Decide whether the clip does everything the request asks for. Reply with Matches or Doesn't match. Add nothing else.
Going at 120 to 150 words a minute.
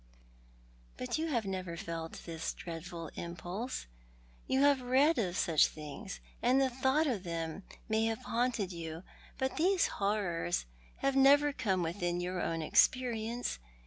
Matches